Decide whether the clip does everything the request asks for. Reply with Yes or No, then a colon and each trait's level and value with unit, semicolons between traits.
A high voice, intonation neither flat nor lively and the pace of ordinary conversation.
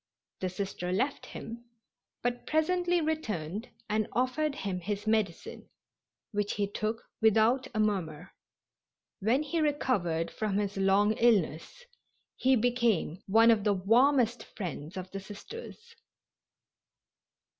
No: high, 215 Hz; average, 4.6 semitones; slow, 120 wpm